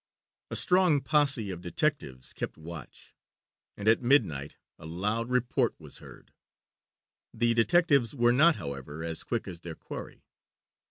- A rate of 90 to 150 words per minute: Yes, average, 140 wpm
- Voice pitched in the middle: No, low, 115 Hz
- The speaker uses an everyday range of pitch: No, wide, 9.0 semitones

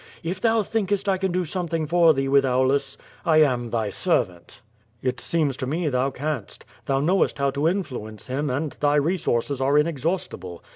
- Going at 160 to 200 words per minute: Yes, average, 190 wpm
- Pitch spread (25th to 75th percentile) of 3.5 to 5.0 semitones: Yes, average, 4.7 semitones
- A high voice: No, medium, 145 Hz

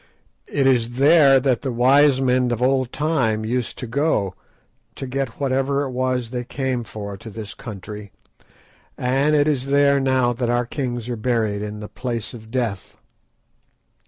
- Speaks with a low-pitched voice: Yes, low, 125 Hz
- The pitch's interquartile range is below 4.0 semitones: Yes, average, 3.0 semitones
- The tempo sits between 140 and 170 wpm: Yes, average, 165 wpm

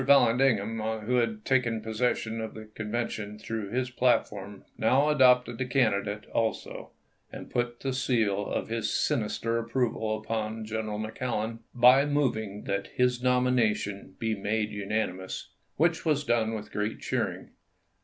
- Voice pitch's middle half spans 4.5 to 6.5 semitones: No, average, 2.8 semitones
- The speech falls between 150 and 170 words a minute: No, slow, 135 wpm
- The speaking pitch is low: Yes, low, 115 Hz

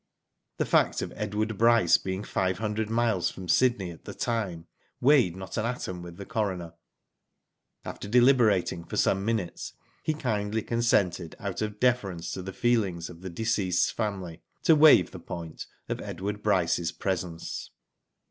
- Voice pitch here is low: Yes, low, 100 Hz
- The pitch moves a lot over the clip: No, average, 4.1 semitones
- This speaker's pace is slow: No, average, 155 wpm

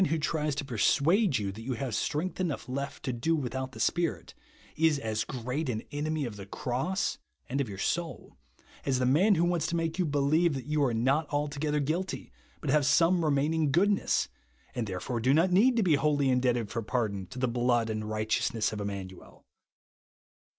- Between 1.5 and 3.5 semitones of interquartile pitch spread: No, average, 5.0 semitones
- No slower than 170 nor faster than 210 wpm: Yes, average, 195 wpm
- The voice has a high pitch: No, medium, 140 Hz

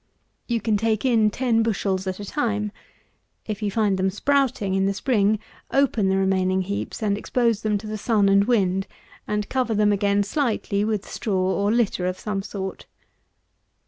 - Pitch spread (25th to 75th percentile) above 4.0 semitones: No, narrow, 2.5 semitones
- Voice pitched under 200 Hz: No, high, 210 Hz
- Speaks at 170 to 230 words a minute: Yes, average, 175 wpm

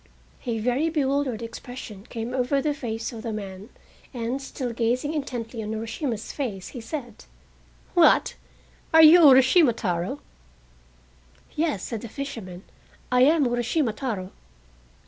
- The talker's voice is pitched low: No, high, 245 Hz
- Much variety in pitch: No, average, 3.9 semitones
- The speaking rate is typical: No, slow, 130 wpm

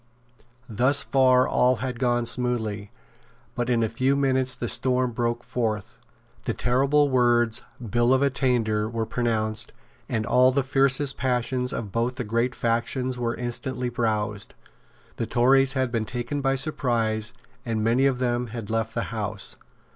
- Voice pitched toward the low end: Yes, low, 120 Hz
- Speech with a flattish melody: Yes, narrow, 2.2 semitones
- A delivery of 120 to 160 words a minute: Yes, average, 155 wpm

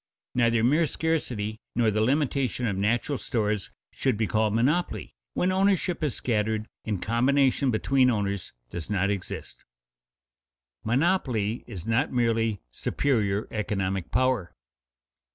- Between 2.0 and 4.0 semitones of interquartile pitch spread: No, average, 4.4 semitones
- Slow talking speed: Yes, slow, 130 wpm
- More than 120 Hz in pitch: No, low, 110 Hz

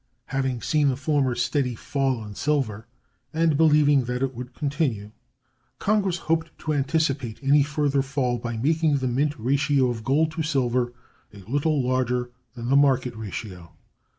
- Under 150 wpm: No, average, 155 wpm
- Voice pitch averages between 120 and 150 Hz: Yes, low, 135 Hz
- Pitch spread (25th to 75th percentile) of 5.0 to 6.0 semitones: No, average, 3.3 semitones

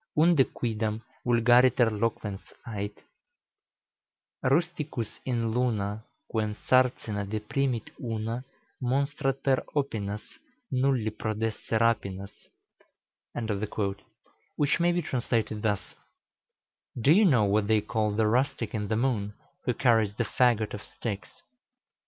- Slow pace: Yes, slow, 110 wpm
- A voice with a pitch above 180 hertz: No, low, 115 Hz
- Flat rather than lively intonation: No, average, 3.4 semitones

